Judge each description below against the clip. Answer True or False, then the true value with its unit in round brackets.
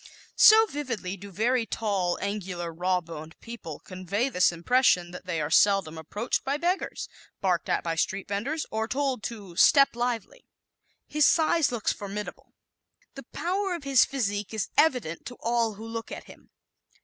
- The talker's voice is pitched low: False (215 Hz)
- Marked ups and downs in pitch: True (6.0 semitones)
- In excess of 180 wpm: False (165 wpm)